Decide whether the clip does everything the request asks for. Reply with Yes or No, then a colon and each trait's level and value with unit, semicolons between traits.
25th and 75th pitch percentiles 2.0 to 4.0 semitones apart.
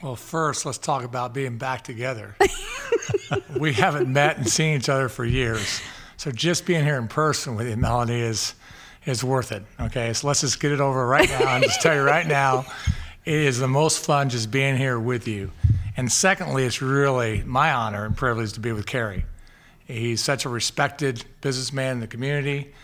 Yes: average, 3.5 semitones